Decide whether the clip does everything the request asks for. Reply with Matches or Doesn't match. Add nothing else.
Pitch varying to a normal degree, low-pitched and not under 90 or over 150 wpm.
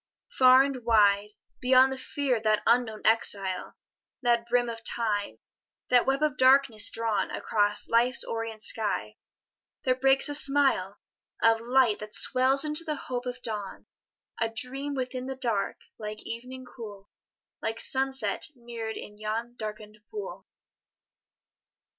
Doesn't match